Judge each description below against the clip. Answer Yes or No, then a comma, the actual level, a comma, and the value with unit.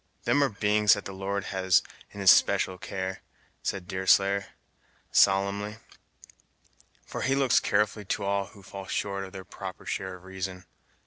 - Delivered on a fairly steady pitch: Yes, narrow, 1.2 semitones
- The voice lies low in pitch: Yes, low, 100 Hz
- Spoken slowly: No, average, 155 wpm